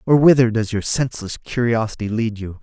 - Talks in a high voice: No, low, 115 Hz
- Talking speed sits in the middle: Yes, average, 185 wpm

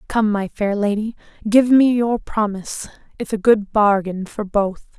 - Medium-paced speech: Yes, average, 170 wpm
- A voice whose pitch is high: Yes, high, 210 Hz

